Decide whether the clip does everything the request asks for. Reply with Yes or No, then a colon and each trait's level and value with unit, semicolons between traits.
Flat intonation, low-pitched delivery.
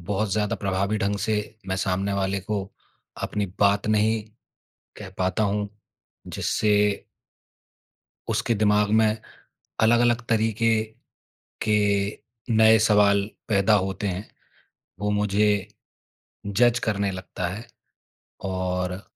Yes: narrow, 1.7 semitones; low, 105 Hz